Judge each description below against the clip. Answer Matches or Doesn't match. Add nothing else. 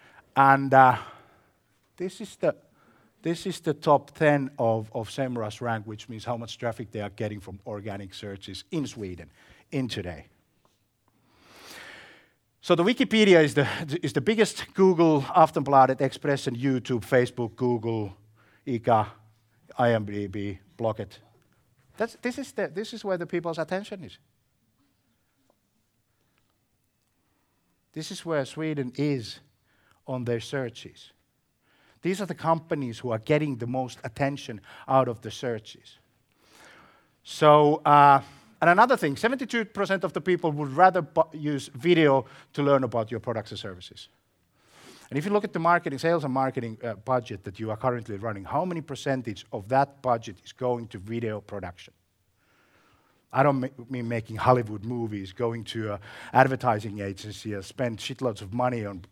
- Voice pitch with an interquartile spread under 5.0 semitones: Doesn't match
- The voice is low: Matches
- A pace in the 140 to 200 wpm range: Matches